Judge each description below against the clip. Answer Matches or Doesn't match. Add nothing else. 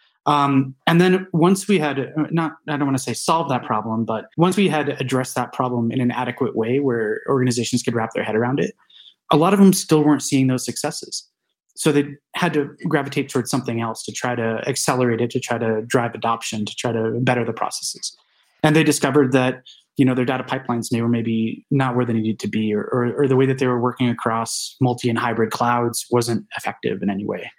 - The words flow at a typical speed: Doesn't match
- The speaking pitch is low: Matches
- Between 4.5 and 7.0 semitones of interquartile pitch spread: Doesn't match